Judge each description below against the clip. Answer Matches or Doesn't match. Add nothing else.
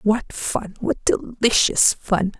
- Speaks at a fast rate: Doesn't match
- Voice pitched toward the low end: Doesn't match